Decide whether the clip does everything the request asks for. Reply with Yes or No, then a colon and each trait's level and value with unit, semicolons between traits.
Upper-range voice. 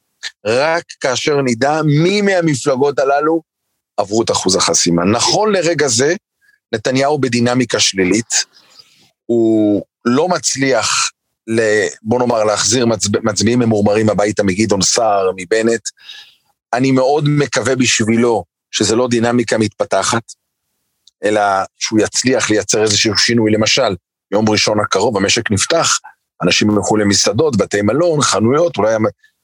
No: low, 120 Hz